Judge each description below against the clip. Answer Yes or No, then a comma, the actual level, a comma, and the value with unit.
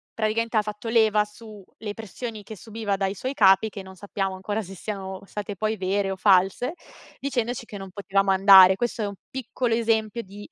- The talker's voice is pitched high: Yes, high, 210 Hz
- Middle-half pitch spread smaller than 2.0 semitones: No, narrow, 2.6 semitones